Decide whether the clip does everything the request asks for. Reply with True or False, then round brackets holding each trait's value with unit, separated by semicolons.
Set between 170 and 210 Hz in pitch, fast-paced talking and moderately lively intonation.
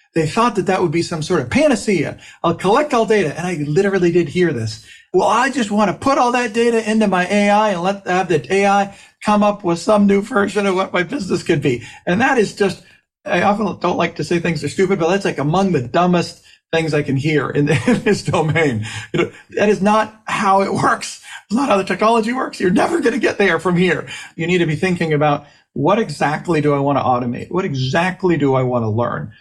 True (185 Hz; 245 wpm; 4.4 semitones)